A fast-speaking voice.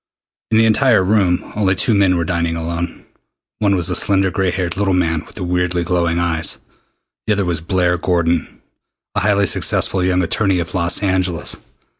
No: average, 180 wpm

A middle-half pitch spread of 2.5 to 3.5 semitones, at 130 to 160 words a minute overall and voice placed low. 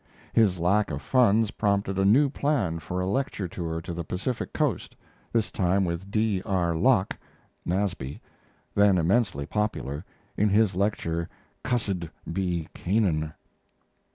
No: average, 3.9 semitones; slow, 135 wpm; very low, 95 Hz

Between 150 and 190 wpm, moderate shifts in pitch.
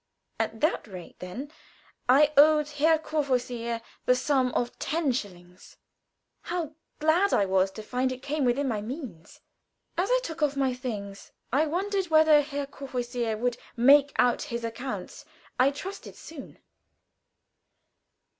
No: average, 140 wpm; average, 4.3 semitones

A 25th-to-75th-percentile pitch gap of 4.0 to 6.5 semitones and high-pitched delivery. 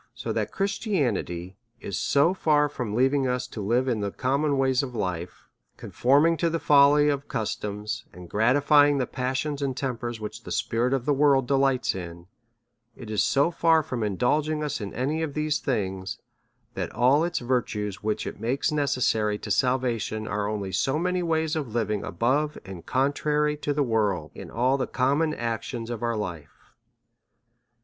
No: average, 5.1 semitones; low, 130 Hz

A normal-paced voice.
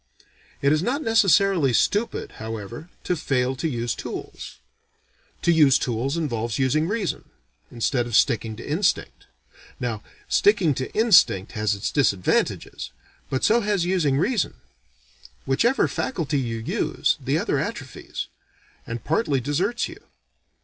No: slow, 130 wpm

